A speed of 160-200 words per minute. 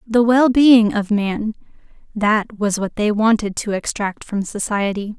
No: average, 150 wpm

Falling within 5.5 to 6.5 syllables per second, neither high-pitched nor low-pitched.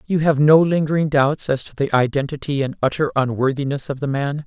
Yes: 5.6 syllables/s; medium, 145 Hz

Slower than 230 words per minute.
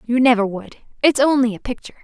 Yes: fast, 205 wpm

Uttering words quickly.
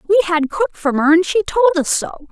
Yes: fast, 260 wpm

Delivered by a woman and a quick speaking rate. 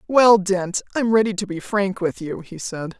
Yes: female; fast, 220 wpm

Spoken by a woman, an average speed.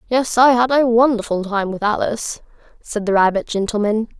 Yes: female; average, 170 wpm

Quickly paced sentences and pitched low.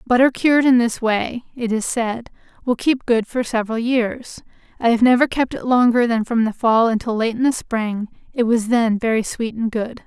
No: fast, 215 wpm; high, 235 Hz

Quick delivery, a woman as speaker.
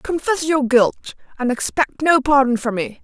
No: average, 180 wpm; female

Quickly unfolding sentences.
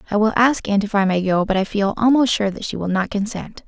Yes: fast, 295 wpm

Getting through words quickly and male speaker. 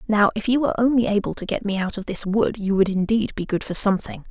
No: fast, 280 wpm; female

